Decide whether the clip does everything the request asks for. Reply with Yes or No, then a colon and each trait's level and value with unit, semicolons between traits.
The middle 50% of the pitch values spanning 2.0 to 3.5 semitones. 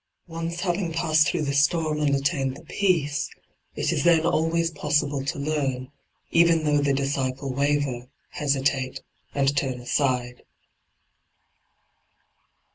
Yes: average, 3.1 semitones